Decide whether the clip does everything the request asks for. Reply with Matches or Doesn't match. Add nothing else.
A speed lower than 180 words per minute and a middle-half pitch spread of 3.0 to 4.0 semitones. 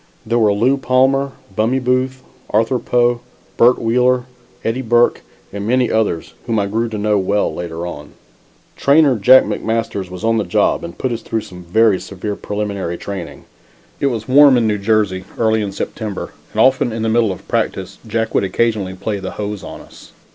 Doesn't match